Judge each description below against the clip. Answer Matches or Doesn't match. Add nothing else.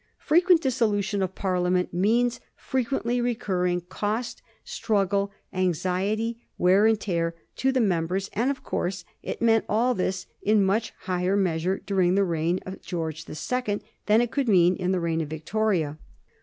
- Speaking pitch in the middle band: Doesn't match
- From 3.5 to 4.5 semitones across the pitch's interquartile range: Matches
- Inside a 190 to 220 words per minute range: Doesn't match